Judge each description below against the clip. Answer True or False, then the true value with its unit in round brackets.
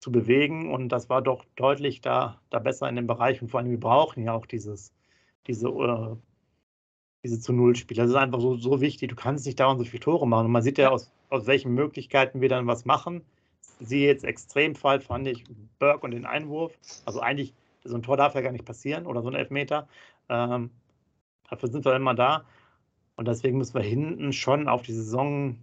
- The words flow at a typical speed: False (215 wpm)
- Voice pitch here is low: True (125 Hz)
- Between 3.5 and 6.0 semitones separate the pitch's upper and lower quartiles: False (2.4 semitones)